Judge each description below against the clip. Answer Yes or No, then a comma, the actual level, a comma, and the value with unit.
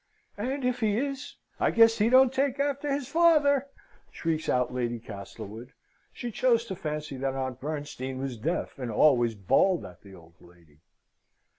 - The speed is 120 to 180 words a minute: Yes, average, 165 wpm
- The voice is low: No, medium, 155 Hz